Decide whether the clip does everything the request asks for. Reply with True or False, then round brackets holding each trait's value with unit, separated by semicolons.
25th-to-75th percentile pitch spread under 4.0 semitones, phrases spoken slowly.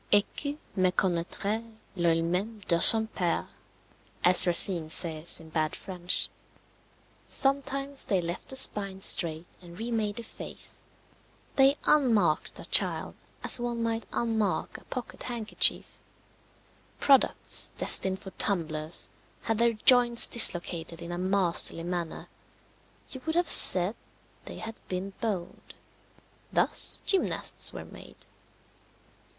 False (5.2 semitones; 120 wpm)